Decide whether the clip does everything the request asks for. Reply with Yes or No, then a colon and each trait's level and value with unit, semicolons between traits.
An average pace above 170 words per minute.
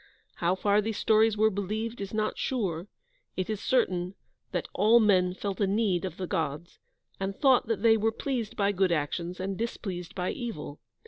Yes: average, 185 wpm